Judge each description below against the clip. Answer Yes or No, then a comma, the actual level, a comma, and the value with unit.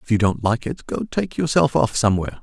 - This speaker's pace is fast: Yes, fast, 245 wpm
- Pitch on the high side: No, low, 110 Hz